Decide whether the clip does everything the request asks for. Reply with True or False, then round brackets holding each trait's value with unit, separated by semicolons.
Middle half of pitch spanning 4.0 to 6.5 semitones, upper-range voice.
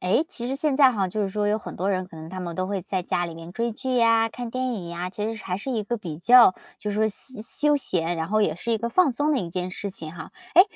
True (4.7 semitones; 210 Hz)